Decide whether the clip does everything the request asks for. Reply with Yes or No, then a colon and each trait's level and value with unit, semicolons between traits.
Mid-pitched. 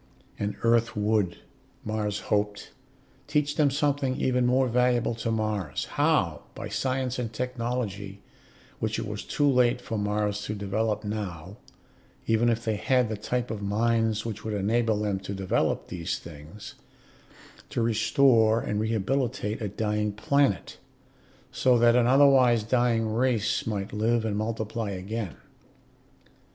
No: low, 110 Hz